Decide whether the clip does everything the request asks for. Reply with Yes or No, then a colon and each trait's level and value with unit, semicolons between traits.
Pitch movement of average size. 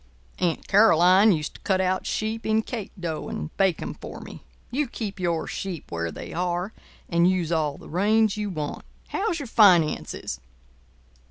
Yes: average, 4.4 semitones